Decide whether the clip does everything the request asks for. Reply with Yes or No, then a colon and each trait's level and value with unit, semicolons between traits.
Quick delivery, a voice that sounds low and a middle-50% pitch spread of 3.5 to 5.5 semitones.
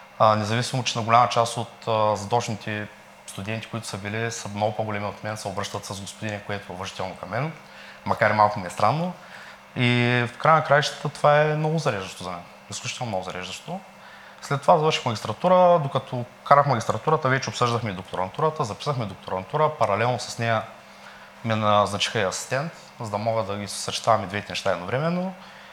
Yes: fast, 175 wpm; low, 110 Hz; average, 4.2 semitones